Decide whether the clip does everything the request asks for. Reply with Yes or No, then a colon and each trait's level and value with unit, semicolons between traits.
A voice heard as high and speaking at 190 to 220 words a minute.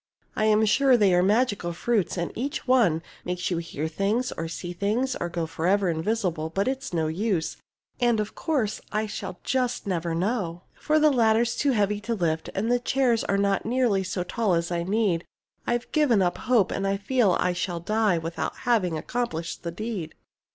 Yes: high, 200 Hz; average, 195 wpm